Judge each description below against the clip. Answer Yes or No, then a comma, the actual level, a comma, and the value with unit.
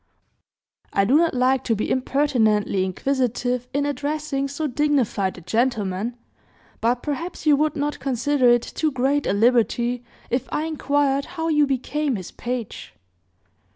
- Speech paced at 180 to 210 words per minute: No, average, 145 wpm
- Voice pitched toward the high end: Yes, very high, 260 Hz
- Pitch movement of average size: Yes, average, 3.5 semitones